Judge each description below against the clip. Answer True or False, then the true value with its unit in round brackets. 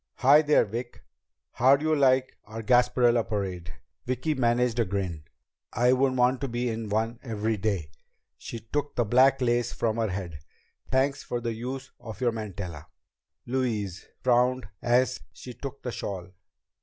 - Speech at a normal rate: True (160 wpm)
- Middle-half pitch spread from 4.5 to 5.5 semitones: False (3.2 semitones)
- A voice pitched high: False (120 Hz)